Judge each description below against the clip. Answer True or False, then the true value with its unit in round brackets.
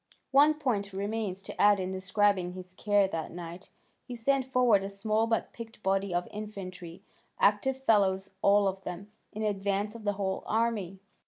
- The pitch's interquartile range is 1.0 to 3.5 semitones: True (2.5 semitones)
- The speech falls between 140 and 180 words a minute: True (170 wpm)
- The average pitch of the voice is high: True (200 Hz)